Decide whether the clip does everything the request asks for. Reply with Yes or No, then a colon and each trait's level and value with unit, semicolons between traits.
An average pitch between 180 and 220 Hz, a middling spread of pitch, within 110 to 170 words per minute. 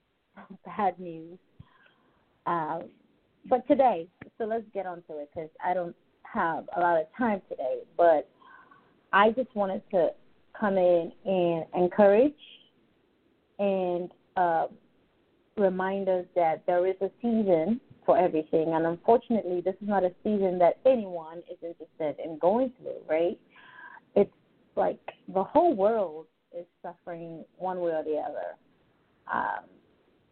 Yes: medium, 185 Hz; average, 4.2 semitones; average, 140 wpm